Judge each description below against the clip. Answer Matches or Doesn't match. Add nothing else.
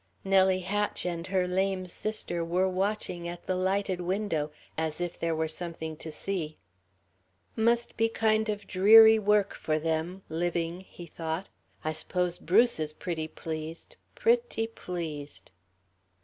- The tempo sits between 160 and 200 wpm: Doesn't match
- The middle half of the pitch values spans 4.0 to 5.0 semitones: Doesn't match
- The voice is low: Doesn't match